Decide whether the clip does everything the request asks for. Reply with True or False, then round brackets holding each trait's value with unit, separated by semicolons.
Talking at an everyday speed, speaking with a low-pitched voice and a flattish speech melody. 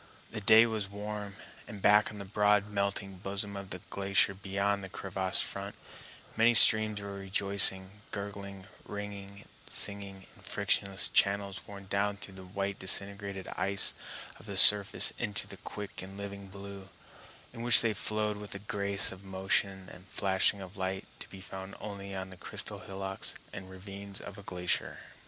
True (165 wpm; 100 Hz; 1.0 semitones)